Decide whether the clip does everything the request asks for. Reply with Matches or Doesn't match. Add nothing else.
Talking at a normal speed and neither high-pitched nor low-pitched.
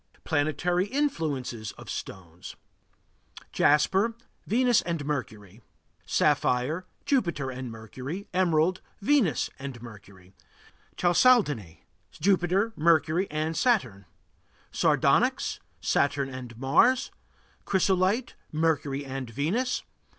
Doesn't match